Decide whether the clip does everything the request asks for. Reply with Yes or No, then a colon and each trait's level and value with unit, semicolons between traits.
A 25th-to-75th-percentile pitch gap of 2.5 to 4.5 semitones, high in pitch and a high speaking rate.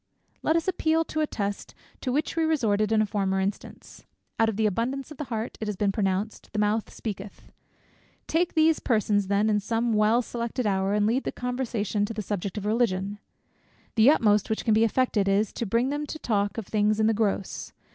Yes: average, 3.3 semitones; high, 220 Hz; fast, 210 wpm